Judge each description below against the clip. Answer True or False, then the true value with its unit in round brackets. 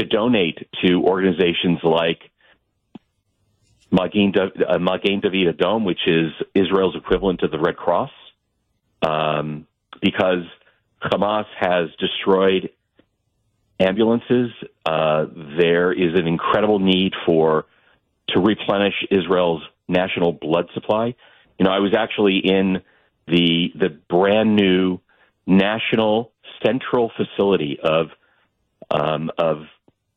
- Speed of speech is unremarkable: False (100 wpm)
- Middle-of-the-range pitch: False (95 Hz)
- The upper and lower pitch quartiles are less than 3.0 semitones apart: False (3.7 semitones)